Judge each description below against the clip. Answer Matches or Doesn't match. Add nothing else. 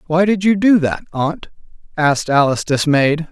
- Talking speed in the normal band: Matches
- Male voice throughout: Matches